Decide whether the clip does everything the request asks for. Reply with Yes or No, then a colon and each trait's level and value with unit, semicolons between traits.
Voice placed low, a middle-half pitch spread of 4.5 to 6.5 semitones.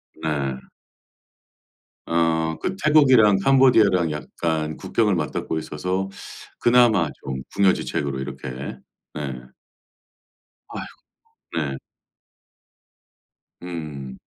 Yes: very low, 80 Hz; average, 5.2 semitones